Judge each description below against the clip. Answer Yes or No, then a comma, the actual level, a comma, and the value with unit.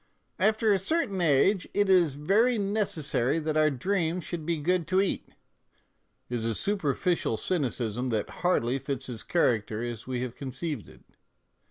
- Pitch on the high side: No, medium, 155 Hz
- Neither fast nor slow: Yes, average, 165 wpm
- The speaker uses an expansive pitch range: Yes, wide, 7.0 semitones